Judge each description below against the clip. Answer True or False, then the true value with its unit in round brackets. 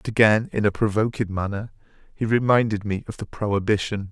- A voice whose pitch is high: False (105 Hz)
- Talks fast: False (175 wpm)